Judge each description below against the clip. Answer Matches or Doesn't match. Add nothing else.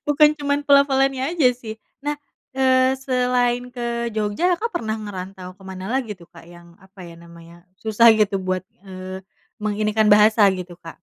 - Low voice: Doesn't match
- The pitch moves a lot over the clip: Matches